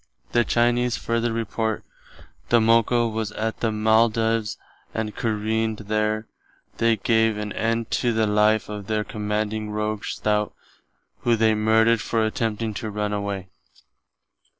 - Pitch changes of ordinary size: No, narrow, 1.2 semitones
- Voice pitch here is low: Yes, low, 110 Hz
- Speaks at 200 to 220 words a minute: No, average, 140 wpm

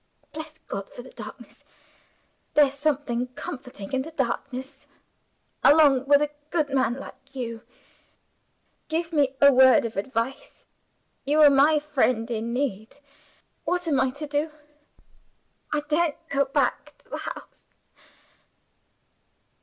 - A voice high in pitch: Yes, very high, 275 Hz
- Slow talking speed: Yes, slow, 130 wpm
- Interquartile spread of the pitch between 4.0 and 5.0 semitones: No, average, 2.9 semitones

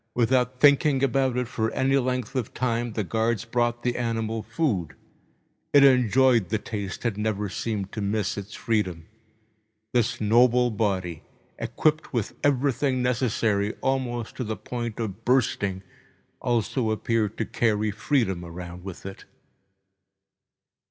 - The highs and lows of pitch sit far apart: No, average, 3.3 semitones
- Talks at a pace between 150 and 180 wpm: No, slow, 135 wpm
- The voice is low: Yes, low, 115 Hz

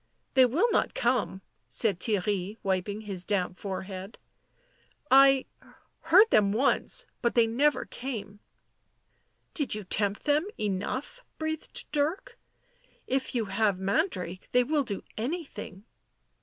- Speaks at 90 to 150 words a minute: Yes, average, 140 wpm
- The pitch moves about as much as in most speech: No, wide, 6.2 semitones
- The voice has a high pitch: Yes, high, 225 Hz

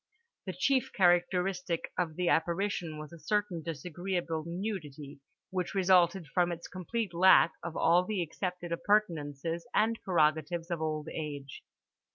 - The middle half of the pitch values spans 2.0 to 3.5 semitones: Yes, average, 2.7 semitones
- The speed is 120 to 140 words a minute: Yes, slow, 135 wpm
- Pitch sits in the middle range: Yes, medium, 175 Hz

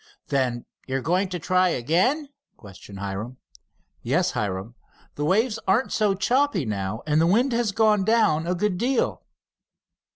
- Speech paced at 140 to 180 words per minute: Yes, average, 155 wpm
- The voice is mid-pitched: Yes, medium, 180 Hz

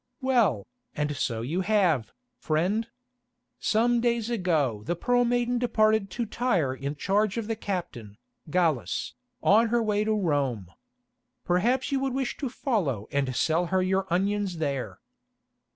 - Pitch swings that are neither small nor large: No, wide, 7.6 semitones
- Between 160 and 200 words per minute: No, average, 145 wpm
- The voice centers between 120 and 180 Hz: No, high, 190 Hz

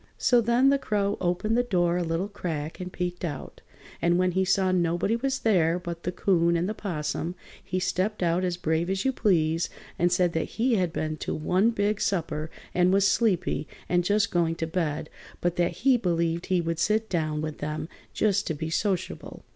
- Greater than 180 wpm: Yes, average, 200 wpm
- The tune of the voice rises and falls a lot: No, average, 3.3 semitones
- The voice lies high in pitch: No, medium, 180 Hz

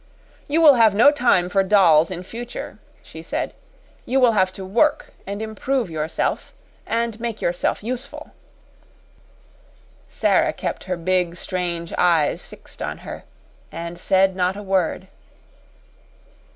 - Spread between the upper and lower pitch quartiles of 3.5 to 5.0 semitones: Yes, average, 4.7 semitones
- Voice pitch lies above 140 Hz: Yes, high, 190 Hz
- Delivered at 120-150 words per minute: Yes, slow, 135 wpm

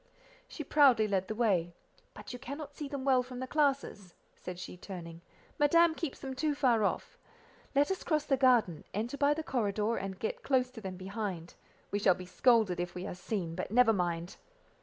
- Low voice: No, high, 230 Hz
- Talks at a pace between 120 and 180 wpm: No, average, 195 wpm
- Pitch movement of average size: No, wide, 6.9 semitones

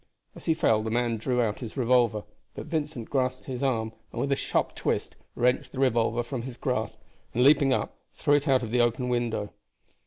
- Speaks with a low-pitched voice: Yes, low, 125 Hz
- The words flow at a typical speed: No, fast, 210 wpm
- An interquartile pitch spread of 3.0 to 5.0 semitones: No, narrow, 2.5 semitones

